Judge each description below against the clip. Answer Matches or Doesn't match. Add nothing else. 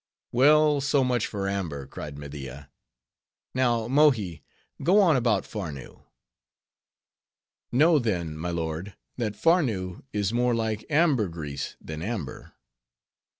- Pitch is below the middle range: Matches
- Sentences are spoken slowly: Matches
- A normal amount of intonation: Doesn't match